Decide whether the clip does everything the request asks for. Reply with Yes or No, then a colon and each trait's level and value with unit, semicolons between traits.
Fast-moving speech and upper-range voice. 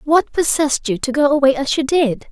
Yes: fast, 235 wpm; very high, 280 Hz